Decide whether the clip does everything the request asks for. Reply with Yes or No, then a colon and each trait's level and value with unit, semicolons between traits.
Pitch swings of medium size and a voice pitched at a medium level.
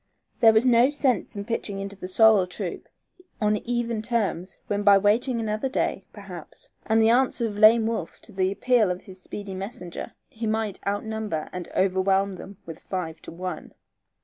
No: average, 3.1 semitones; high, 210 Hz